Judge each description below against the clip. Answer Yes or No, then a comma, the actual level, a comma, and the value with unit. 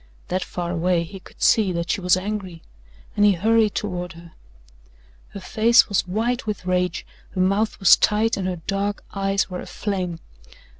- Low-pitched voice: No, high, 190 Hz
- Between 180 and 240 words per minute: No, average, 170 wpm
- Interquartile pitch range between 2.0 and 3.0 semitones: Yes, narrow, 2.6 semitones